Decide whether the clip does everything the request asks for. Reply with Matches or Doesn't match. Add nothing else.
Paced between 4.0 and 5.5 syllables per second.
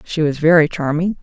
Matches